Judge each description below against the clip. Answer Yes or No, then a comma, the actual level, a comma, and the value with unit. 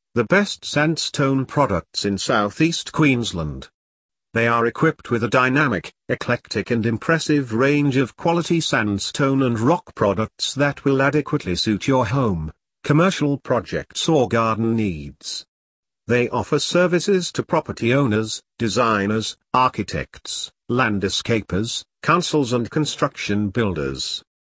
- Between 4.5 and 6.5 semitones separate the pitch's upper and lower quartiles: Yes, average, 5.2 semitones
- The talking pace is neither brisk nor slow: No, slow, 115 wpm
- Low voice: Yes, low, 120 Hz